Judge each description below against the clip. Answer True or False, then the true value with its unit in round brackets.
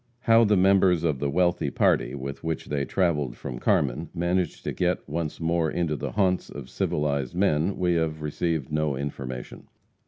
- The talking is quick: False (175 wpm)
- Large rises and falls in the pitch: False (3.8 semitones)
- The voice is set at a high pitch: False (80 Hz)